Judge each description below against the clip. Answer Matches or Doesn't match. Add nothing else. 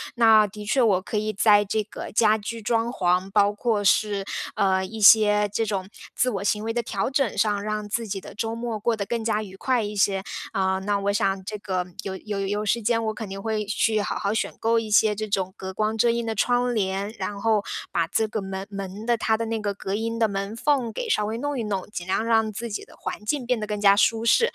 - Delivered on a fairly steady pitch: Matches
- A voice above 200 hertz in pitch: Matches